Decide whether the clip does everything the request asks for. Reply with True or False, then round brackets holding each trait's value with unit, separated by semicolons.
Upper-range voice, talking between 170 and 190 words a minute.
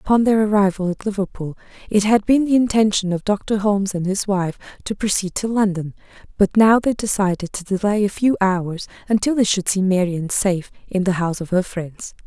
False (200 Hz; 200 wpm)